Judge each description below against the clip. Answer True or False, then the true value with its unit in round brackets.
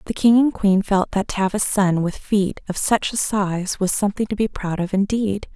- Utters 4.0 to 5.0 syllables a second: True (4.9 syllables/s)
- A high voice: True (200 Hz)